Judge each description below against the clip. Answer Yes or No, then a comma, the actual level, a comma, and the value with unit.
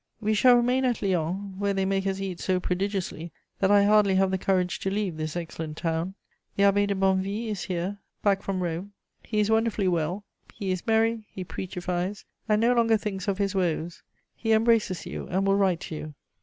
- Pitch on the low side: No, high, 195 Hz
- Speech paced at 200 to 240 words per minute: Yes, fast, 205 wpm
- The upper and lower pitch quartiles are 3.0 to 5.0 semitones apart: No, narrow, 2.5 semitones